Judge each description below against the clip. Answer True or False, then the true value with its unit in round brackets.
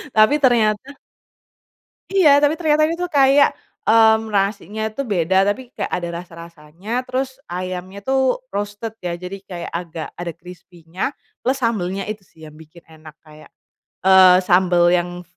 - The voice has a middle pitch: False (195 Hz)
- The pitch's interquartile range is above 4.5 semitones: True (5.6 semitones)